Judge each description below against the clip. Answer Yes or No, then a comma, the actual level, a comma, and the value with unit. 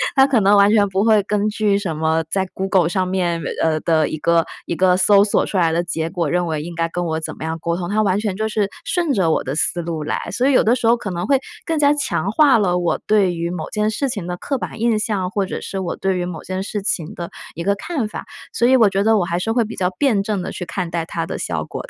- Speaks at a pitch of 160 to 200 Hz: Yes, high, 190 Hz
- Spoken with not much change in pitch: No, average, 3.9 semitones